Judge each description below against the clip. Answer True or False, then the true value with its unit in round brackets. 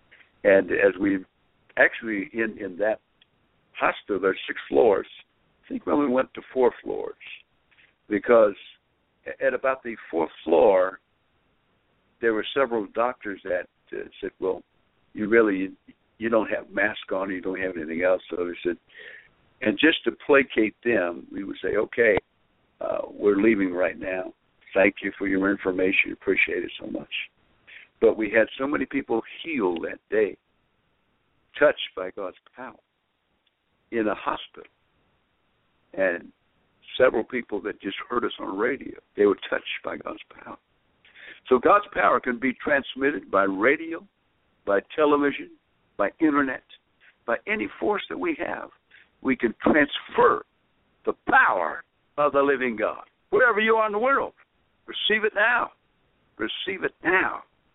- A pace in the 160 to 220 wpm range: False (150 wpm)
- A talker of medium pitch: True (145 Hz)